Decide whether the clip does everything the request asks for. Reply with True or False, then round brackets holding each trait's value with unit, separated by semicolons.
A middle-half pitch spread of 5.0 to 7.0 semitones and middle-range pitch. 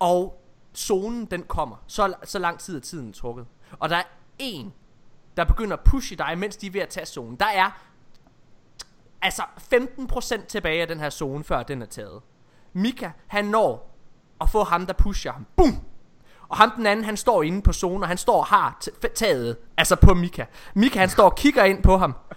True (5.3 semitones; 180 Hz)